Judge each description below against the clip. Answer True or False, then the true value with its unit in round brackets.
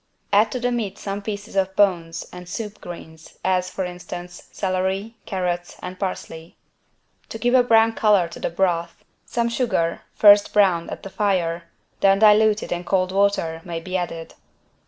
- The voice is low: False (190 Hz)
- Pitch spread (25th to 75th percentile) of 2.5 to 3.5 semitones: True (3.0 semitones)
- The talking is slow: False (165 wpm)